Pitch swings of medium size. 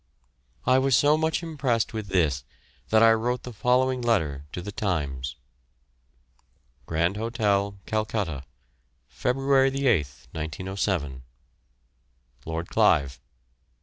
No: wide, 7.6 semitones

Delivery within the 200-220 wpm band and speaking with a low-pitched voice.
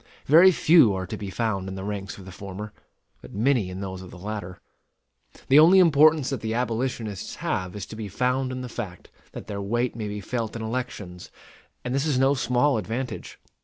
Yes: fast, 205 wpm; low, 110 Hz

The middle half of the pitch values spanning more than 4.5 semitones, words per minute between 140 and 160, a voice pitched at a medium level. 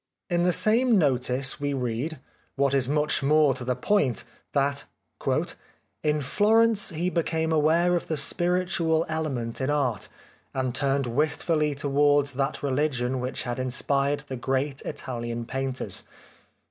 No: average, 3.4 semitones; average, 145 wpm; medium, 145 Hz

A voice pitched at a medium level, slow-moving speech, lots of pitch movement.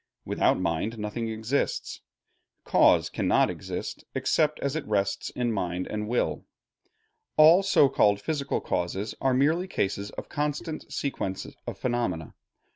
No: low, 115 Hz; slow, 130 wpm; wide, 6.6 semitones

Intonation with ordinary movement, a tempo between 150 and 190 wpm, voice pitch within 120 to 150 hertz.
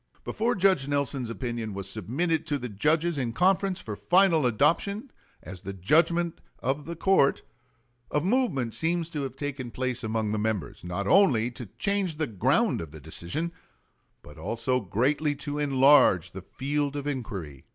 No: wide, 6.8 semitones; average, 160 wpm; medium, 140 Hz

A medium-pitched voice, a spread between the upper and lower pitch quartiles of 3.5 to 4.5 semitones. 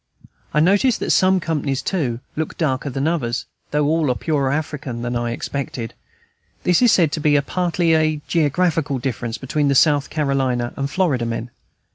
Yes: medium, 145 Hz; average, 3.9 semitones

